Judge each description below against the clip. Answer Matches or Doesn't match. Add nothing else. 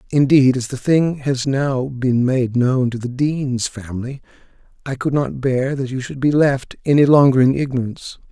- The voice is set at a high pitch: Doesn't match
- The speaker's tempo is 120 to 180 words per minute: Doesn't match